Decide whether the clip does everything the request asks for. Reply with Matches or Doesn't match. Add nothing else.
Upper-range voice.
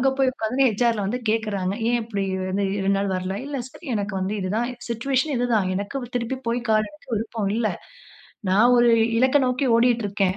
Matches